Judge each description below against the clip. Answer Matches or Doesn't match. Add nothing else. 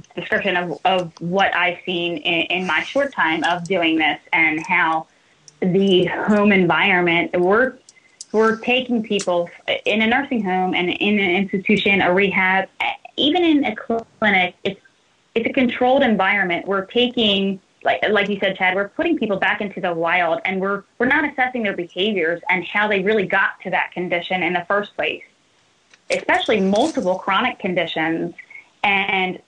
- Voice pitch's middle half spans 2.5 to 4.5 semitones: Matches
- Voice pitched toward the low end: Doesn't match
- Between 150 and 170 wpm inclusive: Matches